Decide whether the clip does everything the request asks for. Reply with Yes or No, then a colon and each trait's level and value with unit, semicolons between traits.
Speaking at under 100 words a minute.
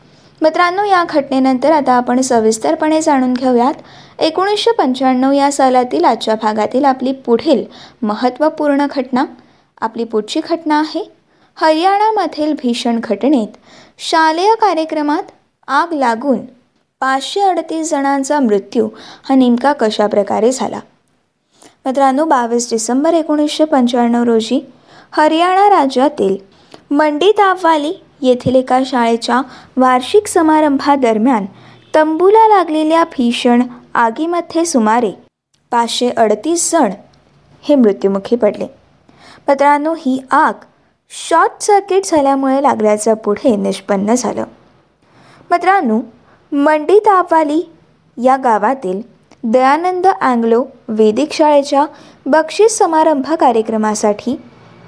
Yes: average, 90 wpm